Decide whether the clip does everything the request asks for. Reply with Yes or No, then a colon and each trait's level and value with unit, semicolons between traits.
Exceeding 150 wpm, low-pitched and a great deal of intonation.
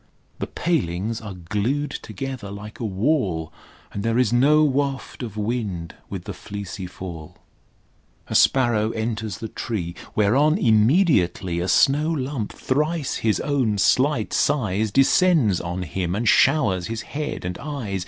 No: average, 145 wpm; low, 110 Hz; wide, 5.9 semitones